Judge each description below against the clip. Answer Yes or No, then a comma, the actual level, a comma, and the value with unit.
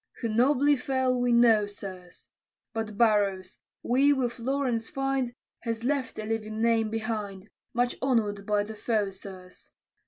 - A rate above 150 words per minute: No, average, 145 wpm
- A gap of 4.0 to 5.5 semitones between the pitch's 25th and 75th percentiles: No, average, 3.2 semitones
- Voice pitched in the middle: No, high, 225 Hz